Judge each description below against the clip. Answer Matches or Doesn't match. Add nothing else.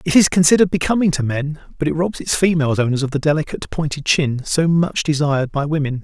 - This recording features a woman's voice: Doesn't match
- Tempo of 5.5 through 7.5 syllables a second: Matches